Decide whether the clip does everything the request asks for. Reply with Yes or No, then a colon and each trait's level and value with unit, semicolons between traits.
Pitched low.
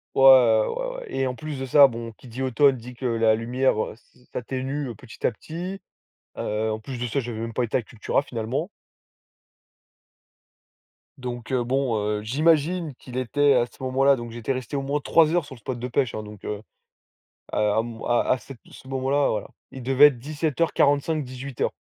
Yes: low, 130 Hz